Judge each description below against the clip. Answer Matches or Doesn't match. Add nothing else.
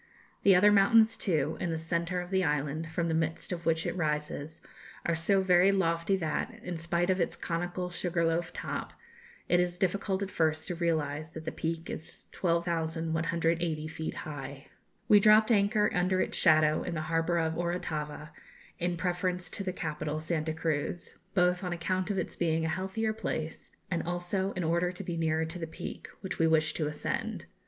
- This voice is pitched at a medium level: Matches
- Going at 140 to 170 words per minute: Doesn't match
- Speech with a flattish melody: Matches